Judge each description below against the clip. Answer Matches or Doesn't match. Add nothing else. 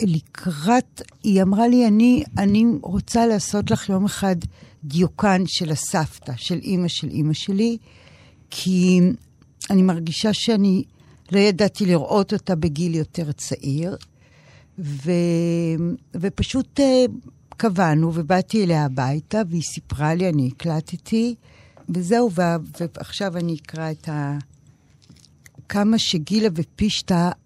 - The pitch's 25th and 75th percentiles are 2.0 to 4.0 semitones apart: Doesn't match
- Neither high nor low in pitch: Matches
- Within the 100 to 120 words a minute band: Matches